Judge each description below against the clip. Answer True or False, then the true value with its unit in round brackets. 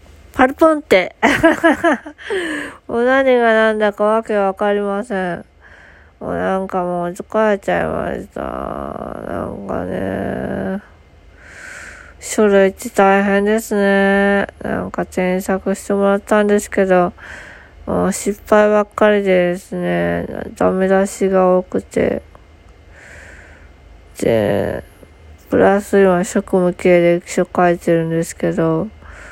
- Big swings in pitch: False (3.5 semitones)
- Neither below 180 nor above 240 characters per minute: True (210 characters per minute)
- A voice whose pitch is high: True (195 Hz)